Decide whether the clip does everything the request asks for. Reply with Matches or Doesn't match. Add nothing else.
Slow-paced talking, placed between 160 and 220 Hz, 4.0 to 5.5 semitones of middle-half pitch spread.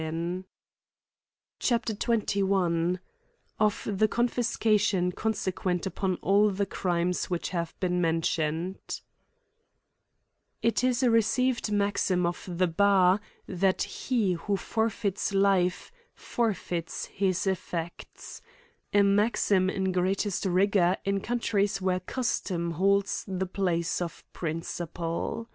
Doesn't match